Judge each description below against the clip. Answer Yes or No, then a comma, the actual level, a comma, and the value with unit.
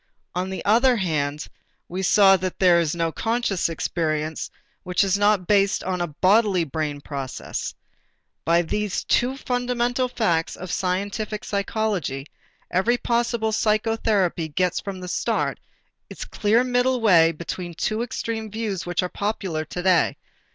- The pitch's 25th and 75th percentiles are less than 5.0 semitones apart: Yes, average, 4.4 semitones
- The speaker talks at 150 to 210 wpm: No, average, 140 wpm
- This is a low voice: No, high, 190 Hz